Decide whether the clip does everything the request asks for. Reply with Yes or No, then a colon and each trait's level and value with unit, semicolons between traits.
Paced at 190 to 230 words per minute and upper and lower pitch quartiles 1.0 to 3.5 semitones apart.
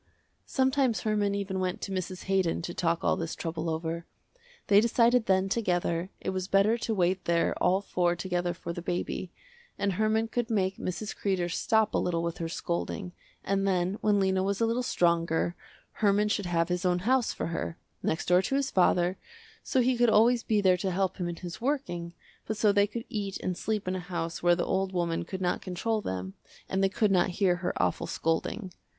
Yes: fast, 205 wpm; average, 3.2 semitones